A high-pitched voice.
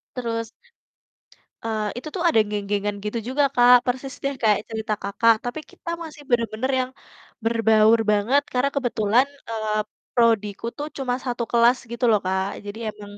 Yes: high, 230 Hz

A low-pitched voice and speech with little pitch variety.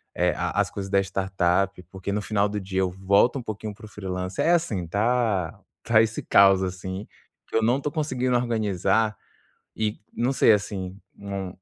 No: low, 100 Hz; average, 3.0 semitones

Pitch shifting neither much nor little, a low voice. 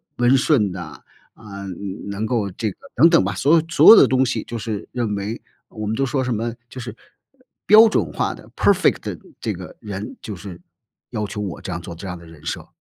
Yes: average, 4.4 semitones; low, 110 Hz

